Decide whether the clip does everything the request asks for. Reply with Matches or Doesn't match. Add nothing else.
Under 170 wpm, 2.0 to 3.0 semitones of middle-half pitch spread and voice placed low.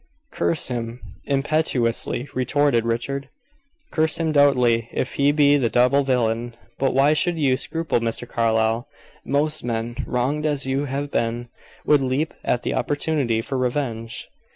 Doesn't match